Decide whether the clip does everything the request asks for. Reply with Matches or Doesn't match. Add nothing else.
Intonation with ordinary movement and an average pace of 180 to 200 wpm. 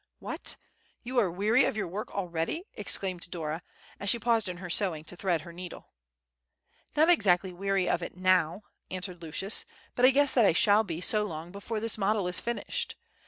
Matches